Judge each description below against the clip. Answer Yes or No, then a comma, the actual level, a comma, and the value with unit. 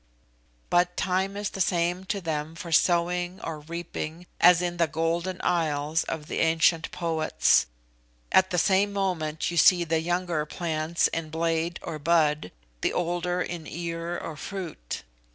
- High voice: No, medium, 170 Hz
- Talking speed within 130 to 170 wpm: Yes, average, 150 wpm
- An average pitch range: No, narrow, 1.7 semitones